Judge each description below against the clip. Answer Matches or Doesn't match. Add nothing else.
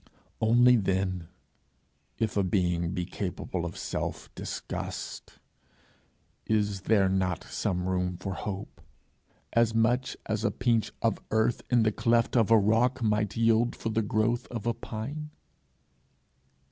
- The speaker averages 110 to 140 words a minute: Matches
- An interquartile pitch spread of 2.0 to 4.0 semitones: Matches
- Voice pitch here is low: Matches